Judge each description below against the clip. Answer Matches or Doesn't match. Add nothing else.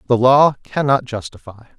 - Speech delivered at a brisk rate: Doesn't match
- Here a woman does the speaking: Doesn't match